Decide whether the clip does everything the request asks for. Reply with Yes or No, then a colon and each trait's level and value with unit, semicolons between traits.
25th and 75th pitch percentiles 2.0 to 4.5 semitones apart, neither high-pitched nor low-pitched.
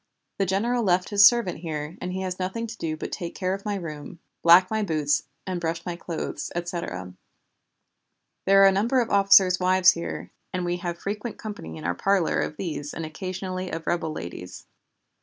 Yes: average, 3.2 semitones; medium, 180 Hz